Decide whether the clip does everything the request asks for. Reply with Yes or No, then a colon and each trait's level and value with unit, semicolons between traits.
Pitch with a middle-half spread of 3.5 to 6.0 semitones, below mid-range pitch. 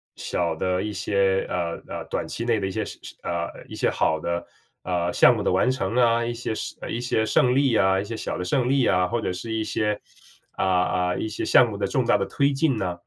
Yes: average, 4.5 semitones; low, 105 Hz